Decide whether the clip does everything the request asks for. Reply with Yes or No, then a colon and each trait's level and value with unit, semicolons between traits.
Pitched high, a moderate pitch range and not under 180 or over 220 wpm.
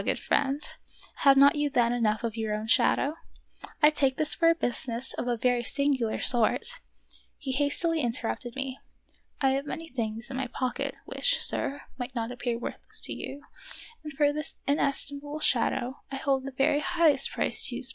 Yes: very high, 270 Hz; average, 3.2 semitones; average, 185 wpm